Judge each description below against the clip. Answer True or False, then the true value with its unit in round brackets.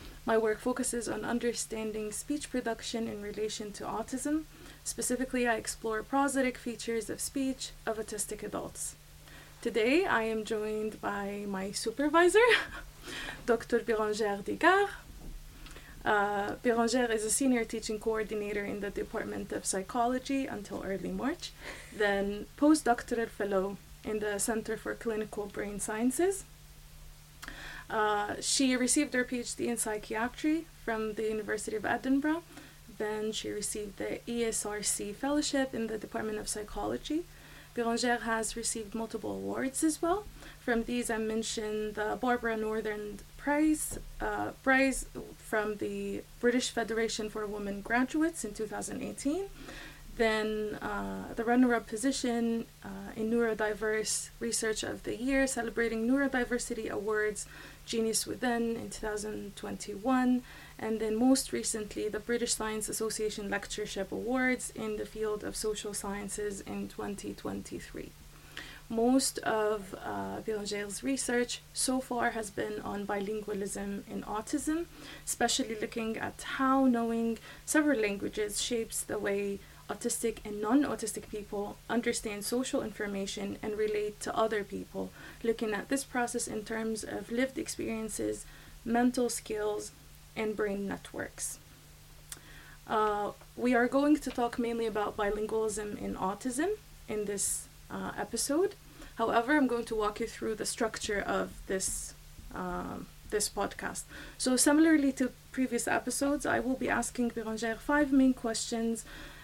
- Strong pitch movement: False (2.8 semitones)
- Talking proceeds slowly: True (130 wpm)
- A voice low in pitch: False (225 Hz)